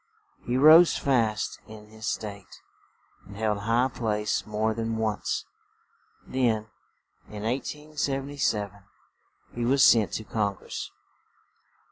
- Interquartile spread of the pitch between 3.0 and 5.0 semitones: Yes, average, 3.5 semitones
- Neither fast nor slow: No, slow, 105 wpm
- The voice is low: Yes, low, 110 Hz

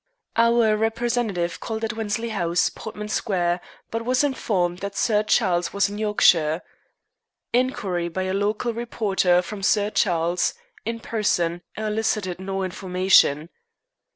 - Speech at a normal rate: No, slow, 125 wpm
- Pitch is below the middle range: No, high, 205 Hz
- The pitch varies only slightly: No, average, 3.8 semitones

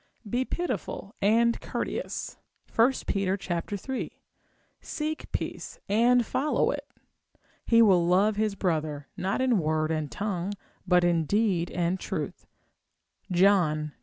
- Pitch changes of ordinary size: Yes, average, 4.8 semitones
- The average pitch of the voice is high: Yes, high, 195 Hz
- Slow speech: Yes, slow, 125 wpm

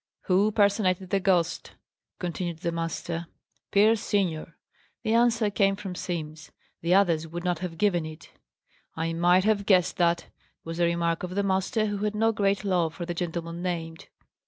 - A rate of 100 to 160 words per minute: No, average, 170 wpm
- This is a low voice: No, medium, 180 Hz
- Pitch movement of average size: Yes, average, 3.1 semitones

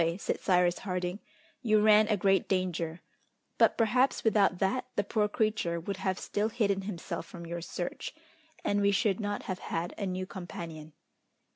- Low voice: No, high, 195 Hz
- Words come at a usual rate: Yes, average, 165 wpm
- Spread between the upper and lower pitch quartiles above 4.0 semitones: No, average, 3.0 semitones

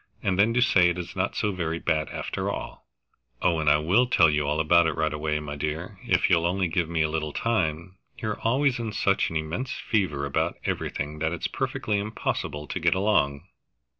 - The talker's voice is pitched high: No, very low, 85 Hz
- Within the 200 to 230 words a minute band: Yes, fast, 205 wpm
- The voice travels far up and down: No, average, 4.3 semitones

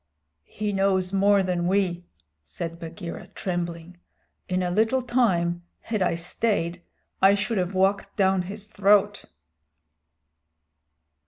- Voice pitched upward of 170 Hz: Yes, high, 190 Hz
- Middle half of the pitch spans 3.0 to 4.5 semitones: No, narrow, 2.6 semitones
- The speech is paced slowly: Yes, slow, 115 wpm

